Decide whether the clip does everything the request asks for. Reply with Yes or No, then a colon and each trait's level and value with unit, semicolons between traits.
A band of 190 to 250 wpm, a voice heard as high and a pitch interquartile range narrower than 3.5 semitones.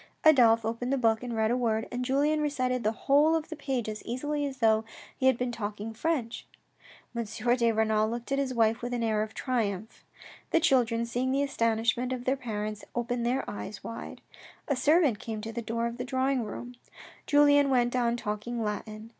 Yes: average, 200 wpm; high, 240 Hz; average, 2.8 semitones